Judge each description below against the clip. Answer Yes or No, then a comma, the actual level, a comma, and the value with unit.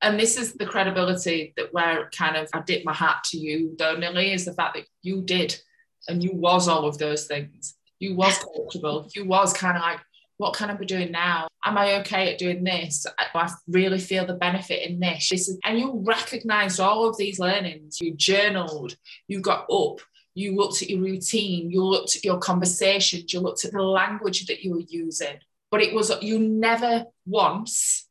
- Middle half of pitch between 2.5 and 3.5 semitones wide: Yes, average, 3.1 semitones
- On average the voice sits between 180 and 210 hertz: Yes, medium, 185 Hz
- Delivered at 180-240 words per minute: Yes, fast, 205 wpm